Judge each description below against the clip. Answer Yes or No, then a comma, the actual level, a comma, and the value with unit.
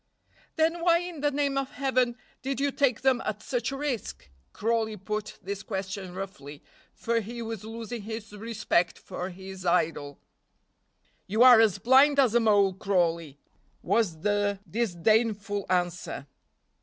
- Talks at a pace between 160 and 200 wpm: No, average, 145 wpm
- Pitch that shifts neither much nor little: Yes, average, 4.8 semitones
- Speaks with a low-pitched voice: No, high, 215 Hz